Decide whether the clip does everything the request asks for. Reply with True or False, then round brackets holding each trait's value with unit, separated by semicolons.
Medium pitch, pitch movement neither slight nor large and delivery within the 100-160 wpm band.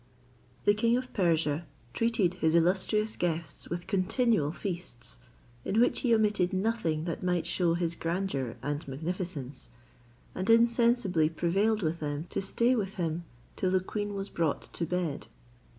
True (180 Hz; 4.4 semitones; 150 wpm)